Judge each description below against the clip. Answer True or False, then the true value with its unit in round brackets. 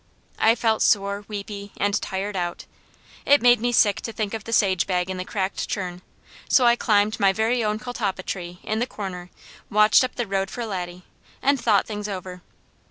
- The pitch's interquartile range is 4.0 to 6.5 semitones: False (2.9 semitones)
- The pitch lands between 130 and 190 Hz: False (205 Hz)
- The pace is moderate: True (195 wpm)